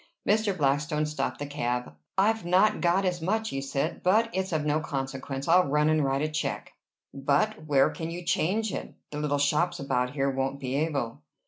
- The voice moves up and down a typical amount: Yes, average, 4.5 semitones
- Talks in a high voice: No, medium, 150 Hz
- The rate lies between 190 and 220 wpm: Yes, average, 195 wpm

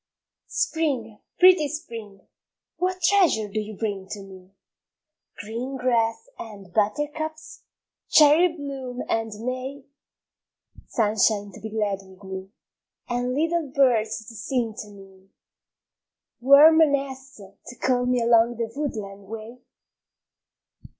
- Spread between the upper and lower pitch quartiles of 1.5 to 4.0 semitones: No, average, 4.9 semitones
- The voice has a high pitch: Yes, high, 235 Hz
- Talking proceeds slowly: Yes, slow, 115 wpm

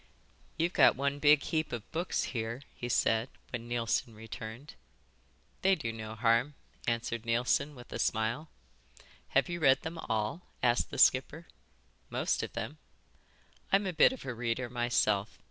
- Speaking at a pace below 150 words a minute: No, average, 155 wpm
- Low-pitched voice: Yes, low, 120 Hz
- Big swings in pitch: No, average, 4.5 semitones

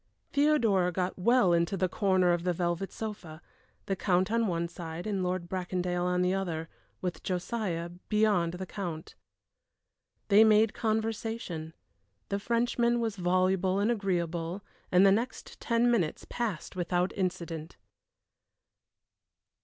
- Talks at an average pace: No, slow, 130 wpm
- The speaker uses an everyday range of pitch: Yes, average, 3.5 semitones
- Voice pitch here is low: No, medium, 185 Hz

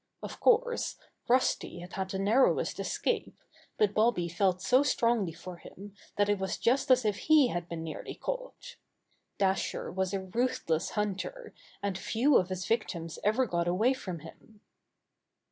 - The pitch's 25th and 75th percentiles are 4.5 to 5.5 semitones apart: Yes, average, 5.2 semitones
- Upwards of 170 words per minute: No, average, 160 wpm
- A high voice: Yes, high, 200 Hz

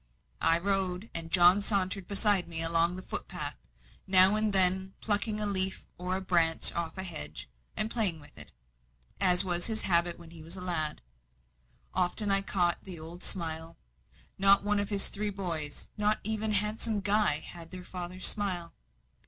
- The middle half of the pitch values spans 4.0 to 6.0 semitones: No, average, 3.0 semitones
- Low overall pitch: No, medium, 185 Hz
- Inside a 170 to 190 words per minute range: No, average, 160 wpm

